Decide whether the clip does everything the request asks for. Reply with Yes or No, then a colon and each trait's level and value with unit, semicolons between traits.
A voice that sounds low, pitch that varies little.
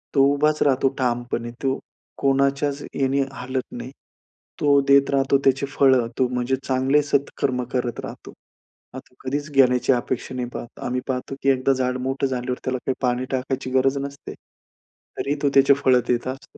Yes: low, 130 Hz; narrow, 1.4 semitones